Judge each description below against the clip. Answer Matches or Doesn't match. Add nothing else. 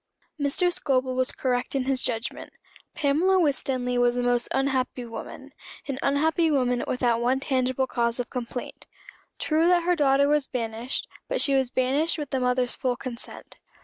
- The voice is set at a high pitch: Matches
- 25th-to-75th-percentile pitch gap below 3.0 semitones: Matches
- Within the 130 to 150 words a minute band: Doesn't match